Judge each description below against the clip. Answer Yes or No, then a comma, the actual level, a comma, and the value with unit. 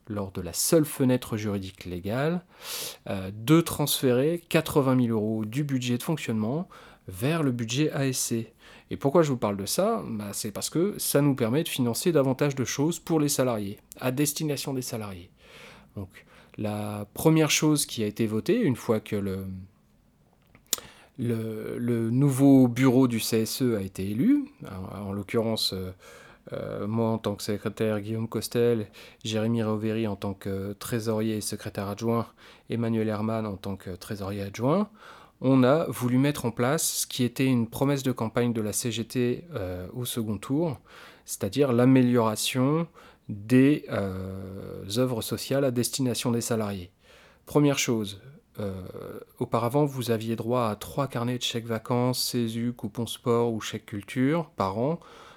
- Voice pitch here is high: No, low, 115 Hz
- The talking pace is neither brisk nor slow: Yes, average, 160 wpm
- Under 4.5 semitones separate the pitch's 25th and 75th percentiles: Yes, average, 4.0 semitones